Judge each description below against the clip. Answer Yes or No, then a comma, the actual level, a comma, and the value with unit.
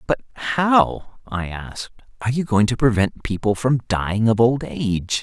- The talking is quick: No, average, 170 wpm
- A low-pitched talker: Yes, low, 115 Hz